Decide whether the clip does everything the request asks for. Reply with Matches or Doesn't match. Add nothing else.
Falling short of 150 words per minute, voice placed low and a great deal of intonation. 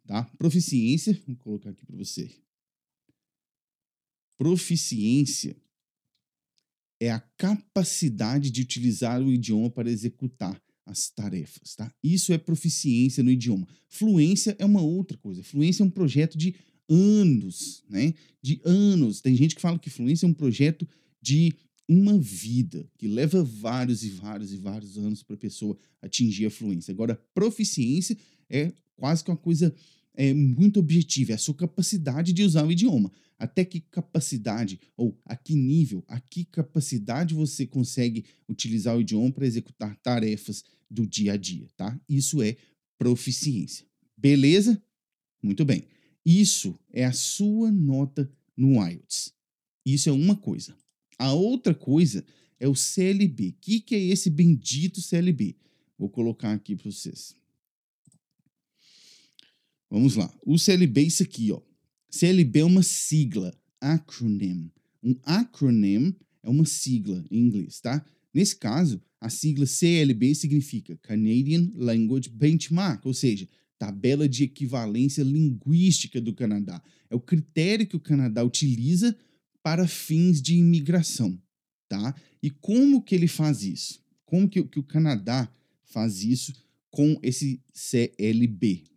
Doesn't match